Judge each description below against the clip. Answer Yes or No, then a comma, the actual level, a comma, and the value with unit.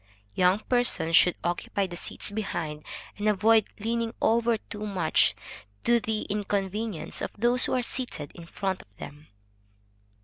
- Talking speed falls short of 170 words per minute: Yes, average, 145 wpm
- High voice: Yes, high, 205 Hz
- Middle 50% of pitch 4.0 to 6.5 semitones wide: Yes, average, 4.3 semitones